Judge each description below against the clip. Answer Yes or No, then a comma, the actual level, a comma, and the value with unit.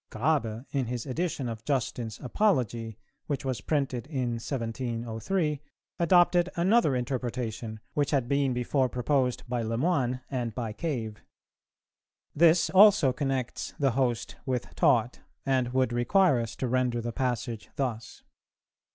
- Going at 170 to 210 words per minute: No, slow, 135 wpm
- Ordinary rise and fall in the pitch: Yes, average, 3.3 semitones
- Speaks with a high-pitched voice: No, low, 125 Hz